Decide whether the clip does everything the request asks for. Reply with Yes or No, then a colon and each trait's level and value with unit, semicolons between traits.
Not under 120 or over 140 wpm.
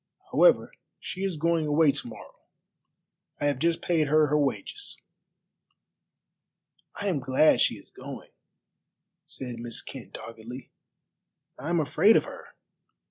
Yes: slow, 135 wpm